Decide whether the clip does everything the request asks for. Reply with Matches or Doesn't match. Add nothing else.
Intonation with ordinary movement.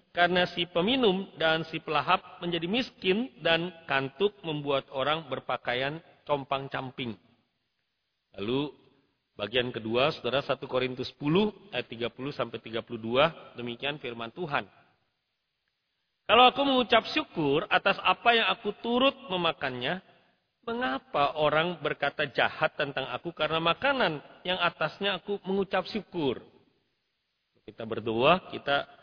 Doesn't match